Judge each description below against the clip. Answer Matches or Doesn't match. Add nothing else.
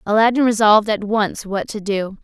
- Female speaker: Matches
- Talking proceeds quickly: Doesn't match